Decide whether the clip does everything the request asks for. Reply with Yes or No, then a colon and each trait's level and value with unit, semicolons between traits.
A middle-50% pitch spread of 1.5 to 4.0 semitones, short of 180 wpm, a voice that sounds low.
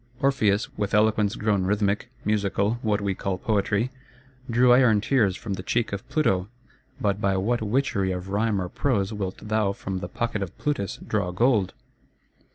Yes: average, 2.8 semitones; average, 165 wpm; low, 105 Hz